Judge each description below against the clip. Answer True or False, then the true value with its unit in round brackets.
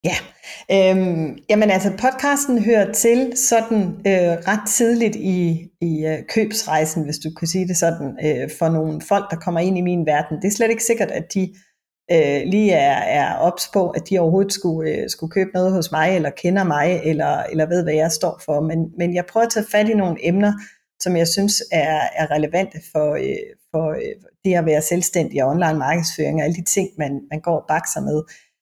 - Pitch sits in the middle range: True (180 Hz)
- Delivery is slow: False (210 wpm)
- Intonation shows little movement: False (4.0 semitones)